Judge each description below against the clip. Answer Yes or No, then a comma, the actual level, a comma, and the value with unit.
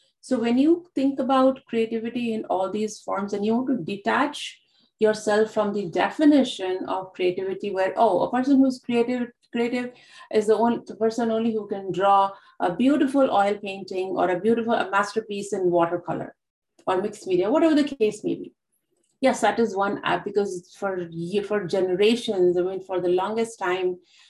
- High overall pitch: Yes, high, 215 Hz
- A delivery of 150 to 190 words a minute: Yes, average, 175 wpm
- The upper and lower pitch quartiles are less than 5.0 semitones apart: Yes, average, 3.9 semitones